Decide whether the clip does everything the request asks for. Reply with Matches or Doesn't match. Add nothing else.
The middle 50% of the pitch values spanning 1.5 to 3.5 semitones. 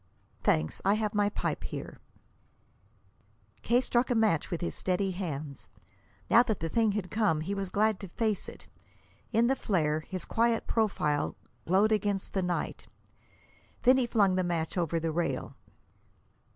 Doesn't match